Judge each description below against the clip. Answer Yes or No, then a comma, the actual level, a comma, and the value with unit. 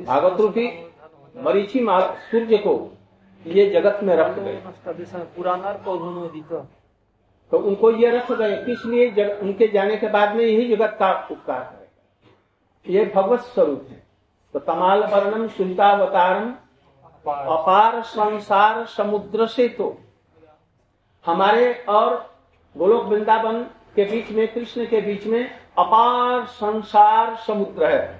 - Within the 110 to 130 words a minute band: Yes, average, 115 wpm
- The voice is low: No, high, 210 Hz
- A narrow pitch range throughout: No, average, 3.8 semitones